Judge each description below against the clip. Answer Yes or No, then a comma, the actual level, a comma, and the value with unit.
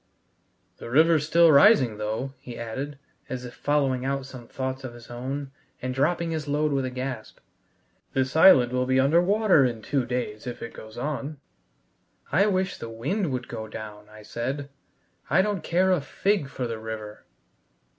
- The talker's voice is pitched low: Yes, low, 130 Hz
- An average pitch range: Yes, average, 4.3 semitones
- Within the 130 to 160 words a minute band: No, average, 175 wpm